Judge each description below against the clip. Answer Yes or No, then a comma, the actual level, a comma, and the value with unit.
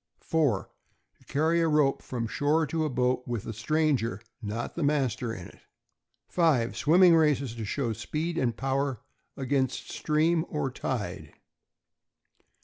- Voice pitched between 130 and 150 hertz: Yes, medium, 140 Hz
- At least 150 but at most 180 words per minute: No, average, 140 wpm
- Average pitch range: Yes, average, 4.8 semitones